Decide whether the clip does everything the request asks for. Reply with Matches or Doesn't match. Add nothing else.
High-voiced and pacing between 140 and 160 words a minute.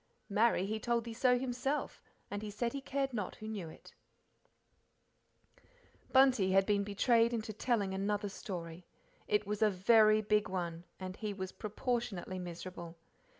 Matches